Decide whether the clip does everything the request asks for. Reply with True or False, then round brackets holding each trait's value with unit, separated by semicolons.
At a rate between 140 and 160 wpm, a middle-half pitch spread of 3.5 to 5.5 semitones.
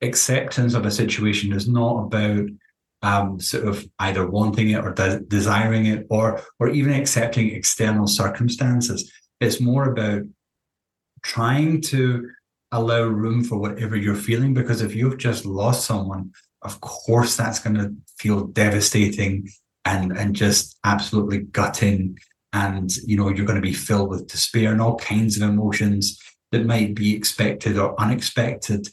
False (150 wpm; 2.5 semitones)